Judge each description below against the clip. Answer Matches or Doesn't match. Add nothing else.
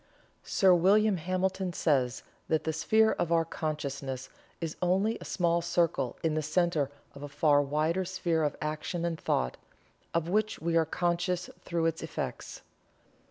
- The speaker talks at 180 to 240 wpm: Doesn't match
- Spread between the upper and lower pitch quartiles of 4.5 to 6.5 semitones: Doesn't match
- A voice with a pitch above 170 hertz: Doesn't match